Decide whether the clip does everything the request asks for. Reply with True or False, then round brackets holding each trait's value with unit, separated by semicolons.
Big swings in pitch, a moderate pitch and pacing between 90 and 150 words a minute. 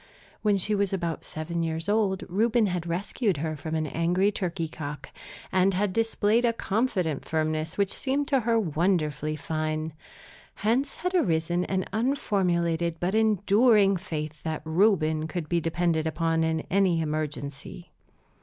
False (4.3 semitones; 175 Hz; 145 wpm)